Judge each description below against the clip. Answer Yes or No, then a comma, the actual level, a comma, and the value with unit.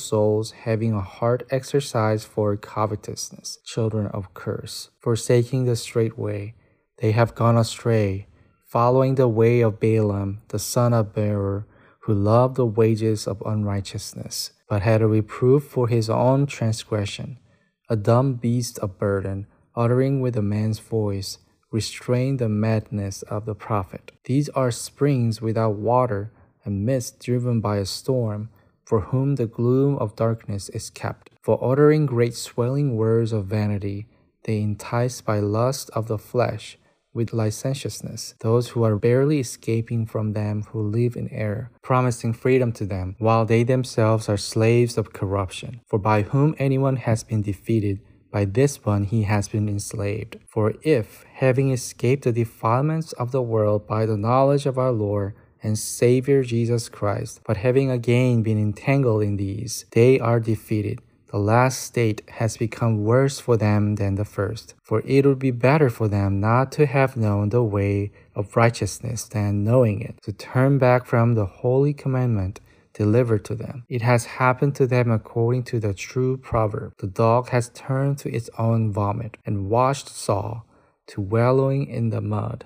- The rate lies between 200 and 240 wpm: No, average, 160 wpm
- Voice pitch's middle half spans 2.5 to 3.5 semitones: Yes, average, 2.9 semitones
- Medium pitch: No, low, 115 Hz